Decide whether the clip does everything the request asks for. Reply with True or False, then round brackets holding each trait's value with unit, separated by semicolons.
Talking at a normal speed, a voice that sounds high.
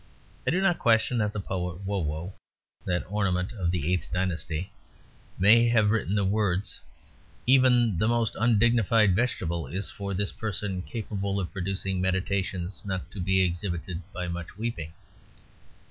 False (150 wpm; 95 Hz)